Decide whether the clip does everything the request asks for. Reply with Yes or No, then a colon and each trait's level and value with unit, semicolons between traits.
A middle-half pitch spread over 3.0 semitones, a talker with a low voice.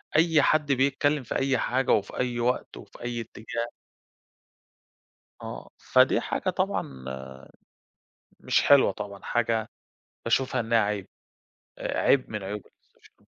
Yes: average, 3.5 semitones; low, 120 Hz